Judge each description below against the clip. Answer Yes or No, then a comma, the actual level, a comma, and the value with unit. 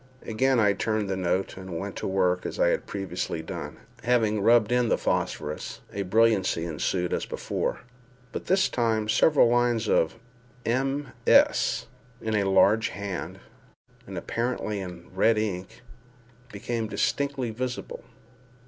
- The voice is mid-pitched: No, low, 110 Hz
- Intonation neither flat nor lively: Yes, average, 4.1 semitones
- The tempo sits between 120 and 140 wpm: Yes, slow, 135 wpm